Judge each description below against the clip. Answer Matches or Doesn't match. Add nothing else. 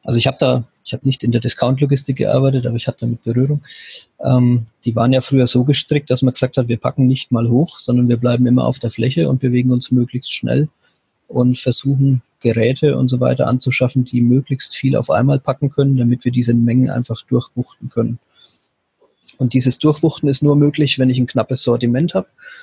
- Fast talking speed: Matches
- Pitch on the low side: Matches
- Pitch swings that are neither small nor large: Doesn't match